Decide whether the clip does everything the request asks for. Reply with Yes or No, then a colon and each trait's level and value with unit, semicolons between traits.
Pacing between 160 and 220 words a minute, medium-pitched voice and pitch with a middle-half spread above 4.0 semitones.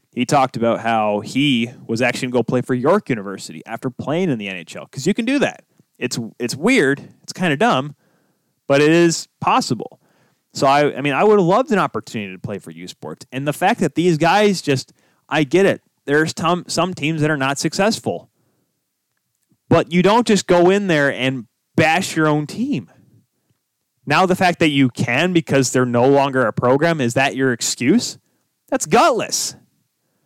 Yes: average, 190 wpm; medium, 145 Hz; wide, 5.5 semitones